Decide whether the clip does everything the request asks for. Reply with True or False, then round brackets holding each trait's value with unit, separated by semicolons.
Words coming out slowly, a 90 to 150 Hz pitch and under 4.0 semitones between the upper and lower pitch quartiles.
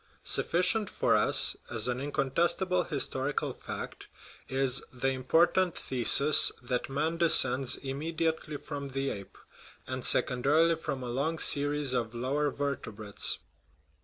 True (125 wpm; 140 Hz; 3.6 semitones)